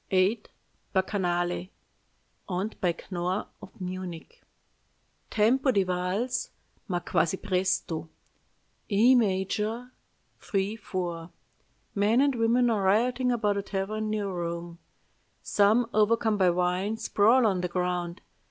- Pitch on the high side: Yes, high, 195 Hz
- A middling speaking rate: No, slow, 115 wpm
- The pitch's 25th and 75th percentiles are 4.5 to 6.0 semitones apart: No, average, 3.5 semitones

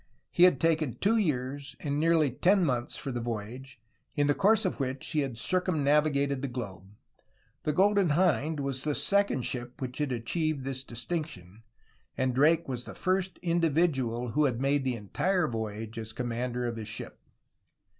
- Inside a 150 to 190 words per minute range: Yes, average, 170 wpm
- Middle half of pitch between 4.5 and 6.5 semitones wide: Yes, average, 5.0 semitones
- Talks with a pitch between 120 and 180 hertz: Yes, medium, 140 Hz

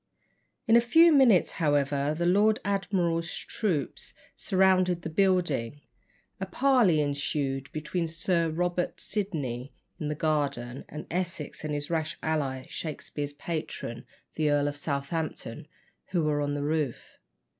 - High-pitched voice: No, medium, 155 Hz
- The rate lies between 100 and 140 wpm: Yes, slow, 135 wpm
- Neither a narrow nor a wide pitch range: Yes, average, 4.0 semitones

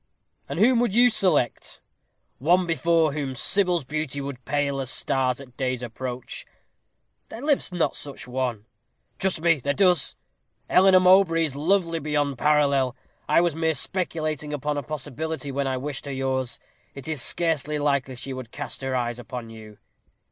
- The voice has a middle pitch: Yes, medium, 145 Hz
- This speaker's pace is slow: No, average, 165 wpm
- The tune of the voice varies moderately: Yes, average, 4.1 semitones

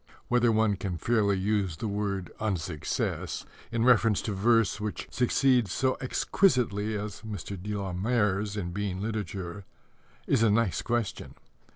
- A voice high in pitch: No, low, 105 Hz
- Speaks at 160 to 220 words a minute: No, average, 145 wpm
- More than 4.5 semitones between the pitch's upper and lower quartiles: No, average, 2.7 semitones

